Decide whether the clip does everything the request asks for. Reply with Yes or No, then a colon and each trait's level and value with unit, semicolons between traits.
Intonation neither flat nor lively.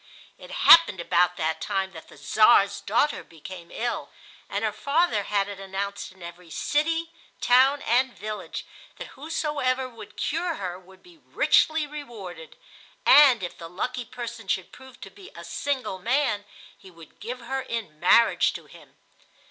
No: wide, 6.0 semitones